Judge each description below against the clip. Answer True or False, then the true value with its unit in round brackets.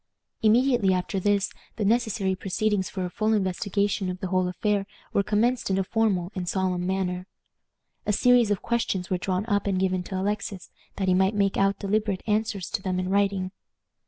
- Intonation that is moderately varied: False (2.1 semitones)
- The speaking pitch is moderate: False (195 Hz)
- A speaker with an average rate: True (190 wpm)